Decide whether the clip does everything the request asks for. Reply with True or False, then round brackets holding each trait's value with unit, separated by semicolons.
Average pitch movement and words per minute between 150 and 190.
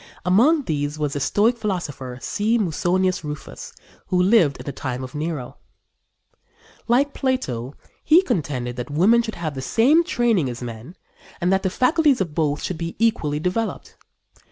False (8.0 semitones; 160 wpm)